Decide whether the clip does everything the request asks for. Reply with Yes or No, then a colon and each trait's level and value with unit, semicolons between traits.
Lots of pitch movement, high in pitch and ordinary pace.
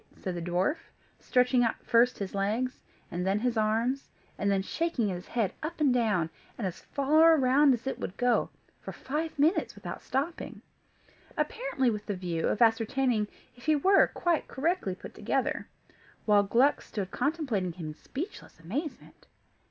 Yes: wide, 6.2 semitones; high, 240 Hz; average, 165 wpm